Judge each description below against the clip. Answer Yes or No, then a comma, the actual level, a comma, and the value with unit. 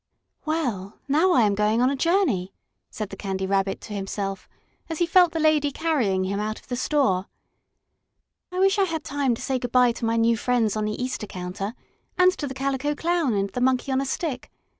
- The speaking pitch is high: Yes, very high, 250 Hz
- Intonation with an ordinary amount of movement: No, wide, 6.6 semitones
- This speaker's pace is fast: Yes, fast, 215 wpm